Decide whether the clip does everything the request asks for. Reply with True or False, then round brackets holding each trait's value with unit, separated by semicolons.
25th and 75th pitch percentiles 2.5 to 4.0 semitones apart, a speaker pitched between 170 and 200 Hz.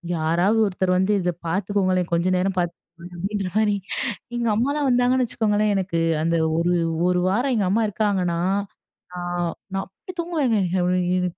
True (3.3 semitones; 190 Hz)